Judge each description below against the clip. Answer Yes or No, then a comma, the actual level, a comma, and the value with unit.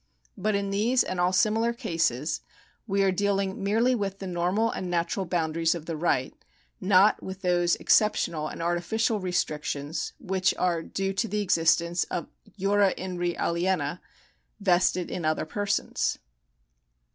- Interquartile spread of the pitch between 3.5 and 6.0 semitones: No, average, 2.9 semitones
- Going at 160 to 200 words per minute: No, average, 145 wpm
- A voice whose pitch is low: No, medium, 185 Hz